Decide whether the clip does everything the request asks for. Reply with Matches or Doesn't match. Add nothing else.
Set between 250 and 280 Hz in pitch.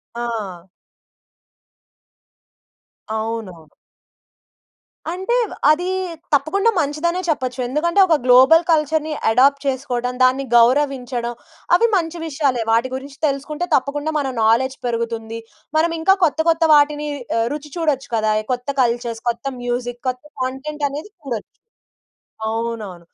Matches